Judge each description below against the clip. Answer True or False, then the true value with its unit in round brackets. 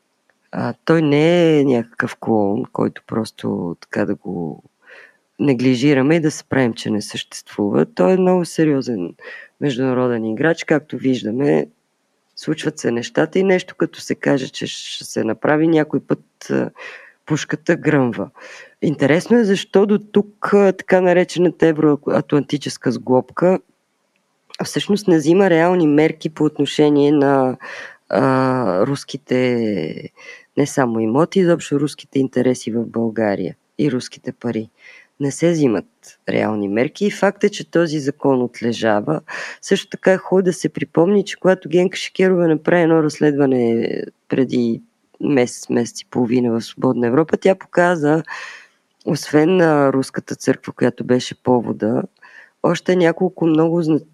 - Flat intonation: False (5.2 semitones)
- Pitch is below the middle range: False (150 Hz)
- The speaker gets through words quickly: False (135 wpm)